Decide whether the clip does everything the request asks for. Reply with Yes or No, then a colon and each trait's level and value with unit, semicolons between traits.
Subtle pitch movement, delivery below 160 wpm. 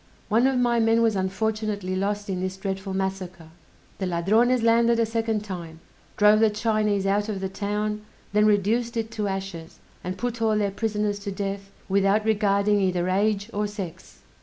No: narrow, 2.2 semitones; average, 175 wpm